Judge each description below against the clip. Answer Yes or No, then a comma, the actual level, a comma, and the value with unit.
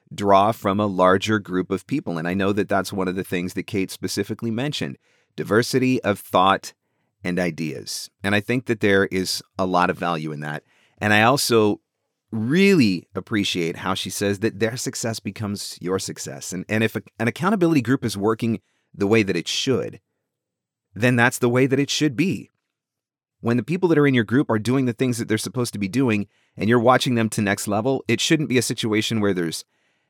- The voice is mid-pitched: No, low, 110 Hz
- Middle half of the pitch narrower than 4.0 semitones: No, average, 4.4 semitones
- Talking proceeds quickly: Yes, fast, 210 wpm